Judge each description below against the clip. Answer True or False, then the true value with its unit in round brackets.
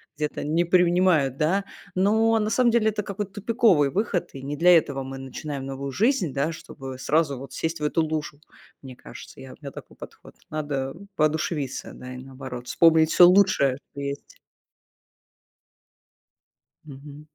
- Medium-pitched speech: True (155 Hz)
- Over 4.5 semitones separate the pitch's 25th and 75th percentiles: True (5.0 semitones)